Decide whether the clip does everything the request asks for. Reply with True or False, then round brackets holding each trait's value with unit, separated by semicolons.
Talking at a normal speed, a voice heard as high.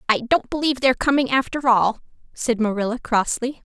True (160 wpm; 245 Hz)